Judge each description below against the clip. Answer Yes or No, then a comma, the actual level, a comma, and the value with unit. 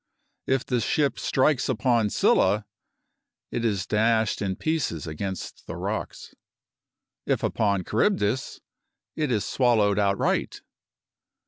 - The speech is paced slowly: Yes, slow, 110 wpm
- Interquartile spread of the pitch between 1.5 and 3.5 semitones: No, average, 4.3 semitones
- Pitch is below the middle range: Yes, low, 110 Hz